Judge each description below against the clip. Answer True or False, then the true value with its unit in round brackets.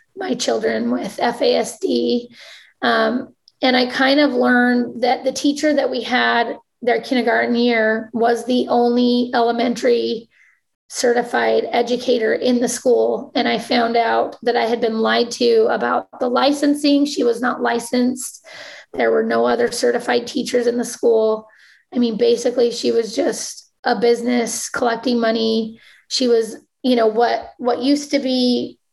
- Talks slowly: False (150 wpm)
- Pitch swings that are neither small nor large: False (1.5 semitones)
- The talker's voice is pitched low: False (240 Hz)